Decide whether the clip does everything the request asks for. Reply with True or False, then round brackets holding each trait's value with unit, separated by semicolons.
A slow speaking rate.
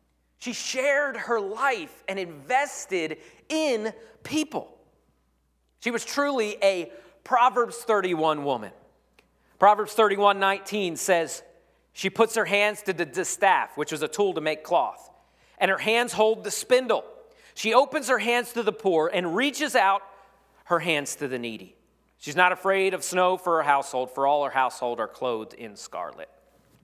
False (155 wpm)